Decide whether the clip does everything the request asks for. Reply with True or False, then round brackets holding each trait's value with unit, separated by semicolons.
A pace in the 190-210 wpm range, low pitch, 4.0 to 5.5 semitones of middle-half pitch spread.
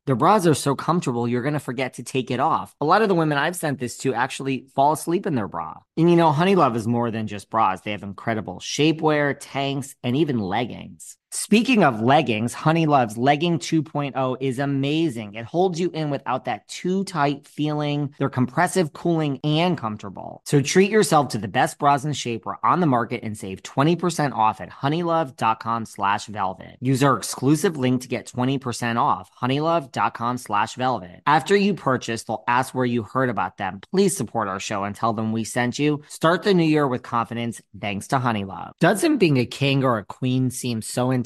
True (200 wpm; 130 Hz; 4.9 semitones)